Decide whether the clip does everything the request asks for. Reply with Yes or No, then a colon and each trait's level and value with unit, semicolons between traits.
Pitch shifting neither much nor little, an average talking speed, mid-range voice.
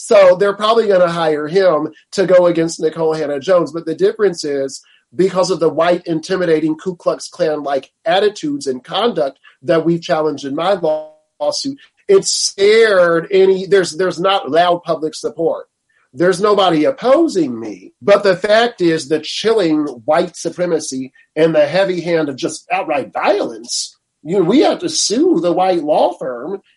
Yes: average, 4.9 semitones; average, 165 wpm; medium, 180 Hz